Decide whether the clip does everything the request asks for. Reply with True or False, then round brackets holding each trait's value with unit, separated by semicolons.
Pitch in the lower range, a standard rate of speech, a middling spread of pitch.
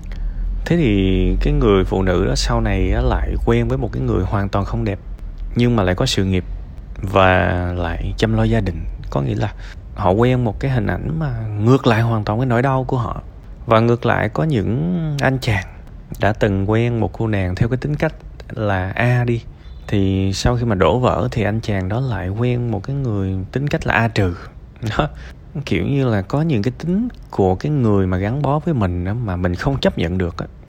True (110 Hz; 225 wpm; 4.6 semitones)